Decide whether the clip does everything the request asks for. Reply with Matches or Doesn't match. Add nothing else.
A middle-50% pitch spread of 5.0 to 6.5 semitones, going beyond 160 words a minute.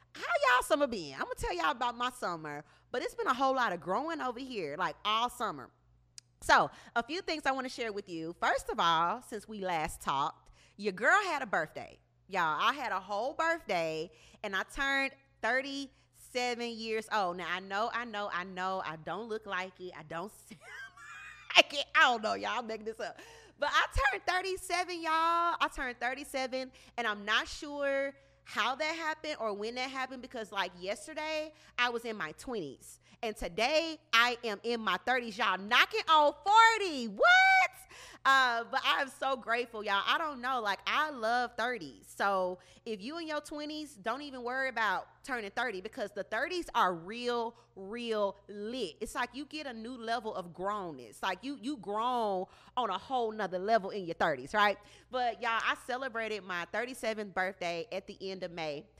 Matches